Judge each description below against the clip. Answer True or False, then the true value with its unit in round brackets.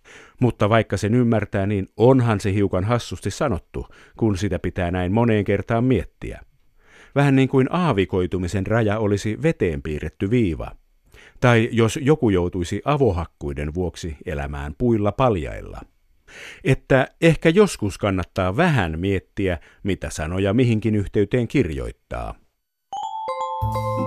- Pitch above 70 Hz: True (105 Hz)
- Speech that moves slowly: False (115 wpm)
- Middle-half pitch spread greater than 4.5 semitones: True (5.5 semitones)